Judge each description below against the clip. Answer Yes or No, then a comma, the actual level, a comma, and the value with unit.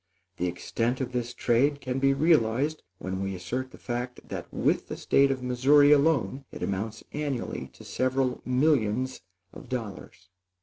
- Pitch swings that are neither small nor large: Yes, average, 3.2 semitones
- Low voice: Yes, low, 125 Hz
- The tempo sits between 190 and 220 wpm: No, average, 160 wpm